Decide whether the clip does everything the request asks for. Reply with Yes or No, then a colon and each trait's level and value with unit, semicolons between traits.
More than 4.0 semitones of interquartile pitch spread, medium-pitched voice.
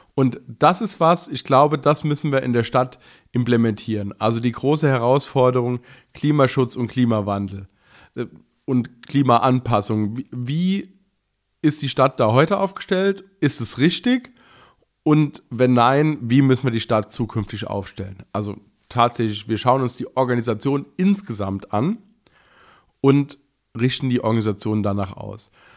No: average, 4.7 semitones; low, 125 Hz